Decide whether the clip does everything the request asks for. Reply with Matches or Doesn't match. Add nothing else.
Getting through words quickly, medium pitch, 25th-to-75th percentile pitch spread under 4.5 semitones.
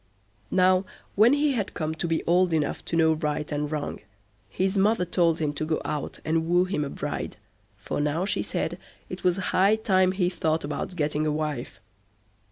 Doesn't match